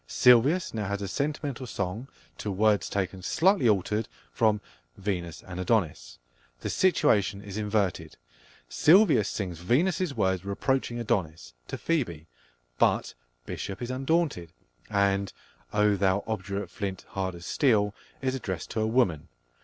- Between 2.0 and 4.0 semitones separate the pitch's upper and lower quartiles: No, average, 4.8 semitones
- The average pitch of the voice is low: Yes, low, 105 Hz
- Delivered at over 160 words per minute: No, slow, 135 wpm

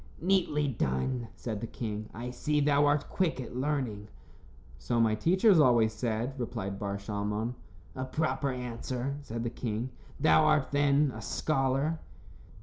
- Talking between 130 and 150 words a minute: Yes, average, 145 wpm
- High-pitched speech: No, low, 125 Hz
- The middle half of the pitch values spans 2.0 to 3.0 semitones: No, average, 4.7 semitones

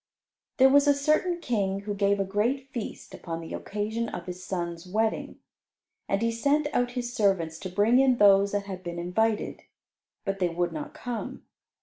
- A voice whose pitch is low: No, high, 205 Hz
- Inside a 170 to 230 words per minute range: Yes, average, 185 wpm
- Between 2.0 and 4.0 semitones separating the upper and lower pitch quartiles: No, average, 4.7 semitones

